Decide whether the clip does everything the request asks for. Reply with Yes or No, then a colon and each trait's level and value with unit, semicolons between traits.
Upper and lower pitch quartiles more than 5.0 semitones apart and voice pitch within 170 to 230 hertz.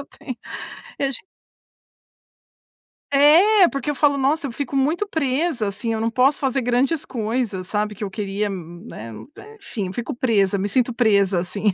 No: wide, 5.5 semitones; high, 240 Hz